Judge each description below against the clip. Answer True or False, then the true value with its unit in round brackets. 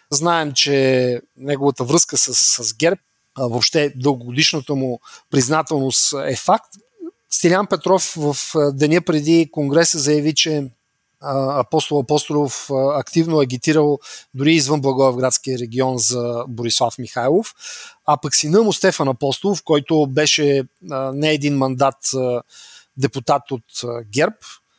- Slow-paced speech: True (115 wpm)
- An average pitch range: True (3.1 semitones)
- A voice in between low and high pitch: True (145 Hz)